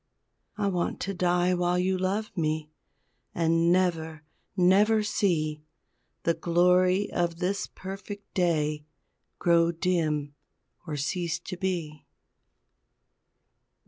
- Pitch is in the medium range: Yes, medium, 175 Hz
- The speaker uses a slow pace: Yes, slow, 105 wpm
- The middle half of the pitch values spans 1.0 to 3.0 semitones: Yes, narrow, 2.4 semitones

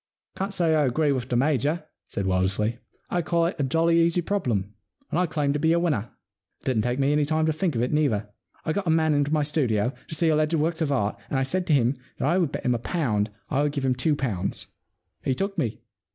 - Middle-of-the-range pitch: Yes, medium, 145 Hz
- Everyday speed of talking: No, fast, 260 wpm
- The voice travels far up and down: No, average, 4.8 semitones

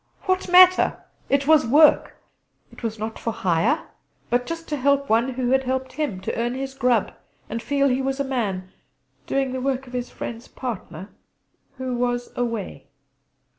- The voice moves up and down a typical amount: Yes, average, 3.0 semitones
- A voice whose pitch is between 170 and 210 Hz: No, very high, 255 Hz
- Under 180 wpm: Yes, average, 170 wpm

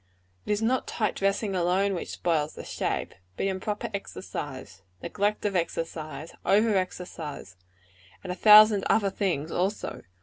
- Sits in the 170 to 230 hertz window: Yes, high, 190 Hz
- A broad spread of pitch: No, average, 4.0 semitones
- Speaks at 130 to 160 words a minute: Yes, average, 140 wpm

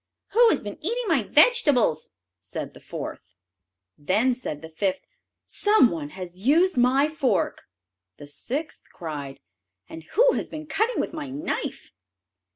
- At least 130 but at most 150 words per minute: Yes, average, 145 wpm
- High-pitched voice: Yes, very high, 255 Hz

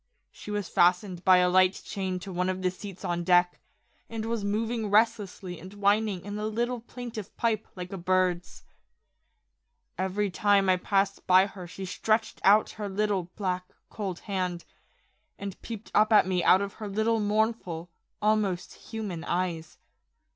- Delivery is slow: No, average, 160 wpm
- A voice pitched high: Yes, high, 195 Hz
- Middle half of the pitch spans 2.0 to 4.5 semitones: Yes, average, 2.7 semitones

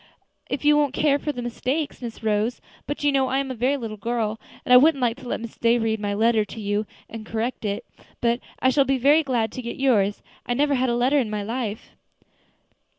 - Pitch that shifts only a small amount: No, average, 3.5 semitones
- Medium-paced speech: No, fast, 240 wpm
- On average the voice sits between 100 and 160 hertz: No, high, 240 Hz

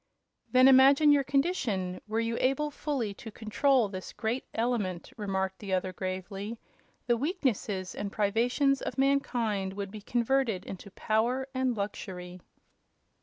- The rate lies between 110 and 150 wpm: Yes, slow, 135 wpm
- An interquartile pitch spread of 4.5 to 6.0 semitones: Yes, average, 5.2 semitones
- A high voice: Yes, high, 225 Hz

